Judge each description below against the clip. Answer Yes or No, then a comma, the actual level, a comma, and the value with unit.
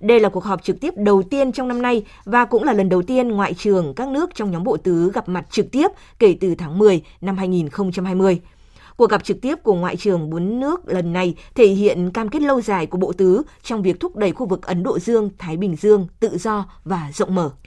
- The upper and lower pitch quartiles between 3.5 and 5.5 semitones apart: Yes, average, 4.0 semitones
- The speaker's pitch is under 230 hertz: Yes, high, 195 Hz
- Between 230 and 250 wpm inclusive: Yes, average, 245 wpm